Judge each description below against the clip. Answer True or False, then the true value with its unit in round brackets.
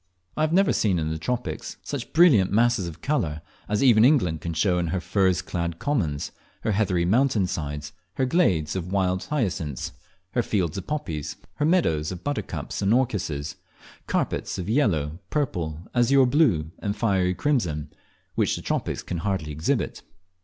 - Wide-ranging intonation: True (7.4 semitones)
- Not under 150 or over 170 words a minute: True (165 wpm)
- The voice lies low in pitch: True (95 Hz)